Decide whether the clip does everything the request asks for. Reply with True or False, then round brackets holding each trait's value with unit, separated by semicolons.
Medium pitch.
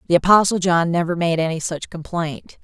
True (170 Hz)